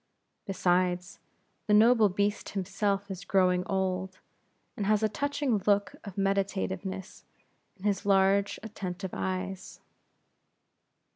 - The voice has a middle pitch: No, high, 195 Hz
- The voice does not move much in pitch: Yes, narrow, 1.7 semitones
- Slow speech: Yes, slow, 110 wpm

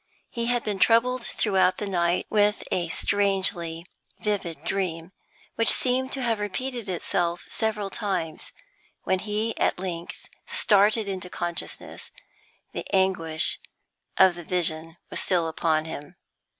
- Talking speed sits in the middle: No, slow, 130 wpm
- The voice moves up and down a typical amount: Yes, average, 3.8 semitones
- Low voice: No, high, 190 Hz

